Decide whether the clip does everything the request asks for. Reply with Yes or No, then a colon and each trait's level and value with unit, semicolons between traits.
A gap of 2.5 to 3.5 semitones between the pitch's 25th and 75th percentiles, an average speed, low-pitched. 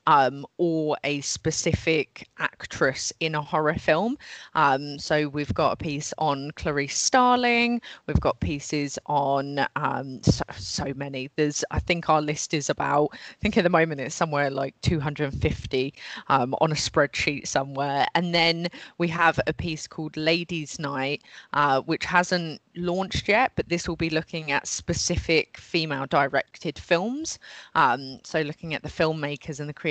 No: average, 2.9 semitones; average, 160 wpm; medium, 150 Hz